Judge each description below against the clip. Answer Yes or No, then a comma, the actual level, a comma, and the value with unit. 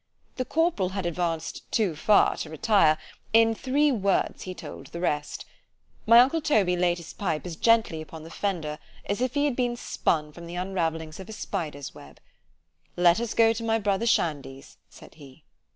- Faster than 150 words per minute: Yes, average, 185 wpm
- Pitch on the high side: No, medium, 180 Hz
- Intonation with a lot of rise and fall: Yes, wide, 6.0 semitones